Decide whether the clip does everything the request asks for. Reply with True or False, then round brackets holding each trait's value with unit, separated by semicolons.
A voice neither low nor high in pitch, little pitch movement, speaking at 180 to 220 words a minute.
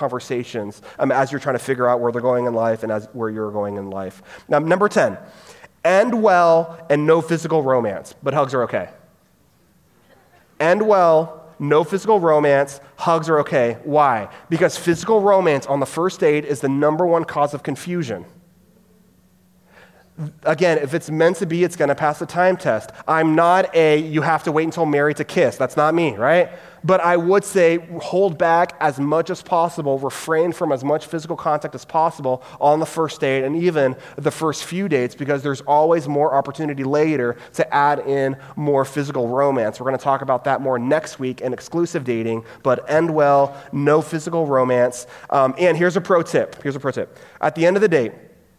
False (150 Hz; 3.7 semitones; 195 wpm)